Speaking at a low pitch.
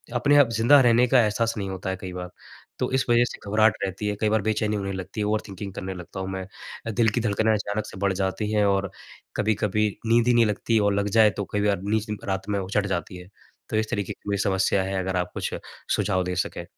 Yes: low, 105 Hz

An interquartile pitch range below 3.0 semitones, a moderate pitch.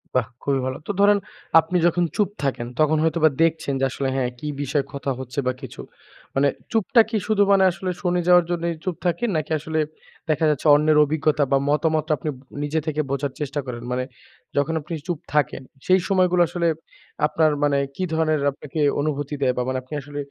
No: average, 3.5 semitones; medium, 155 Hz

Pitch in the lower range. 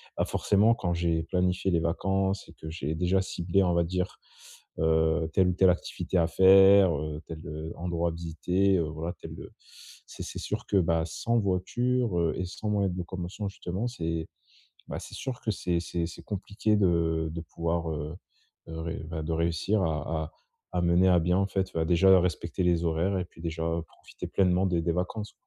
Yes: very low, 85 Hz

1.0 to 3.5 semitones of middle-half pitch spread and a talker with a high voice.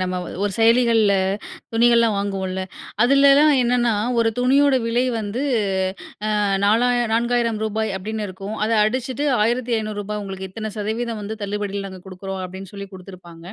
Yes: average, 3.2 semitones; high, 215 Hz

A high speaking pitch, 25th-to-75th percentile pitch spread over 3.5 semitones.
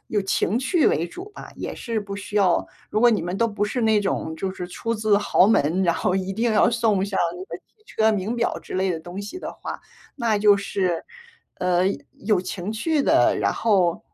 No: high, 205 Hz; average, 3.2 semitones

